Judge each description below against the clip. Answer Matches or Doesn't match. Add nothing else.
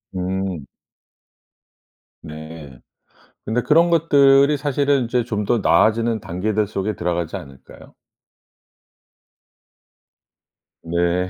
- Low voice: Matches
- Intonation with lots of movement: Matches